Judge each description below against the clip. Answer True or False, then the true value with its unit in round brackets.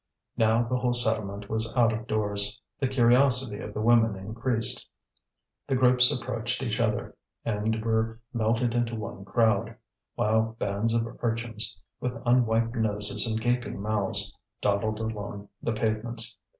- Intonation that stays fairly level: True (1.8 semitones)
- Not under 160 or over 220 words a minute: False (140 wpm)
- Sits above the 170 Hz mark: False (115 Hz)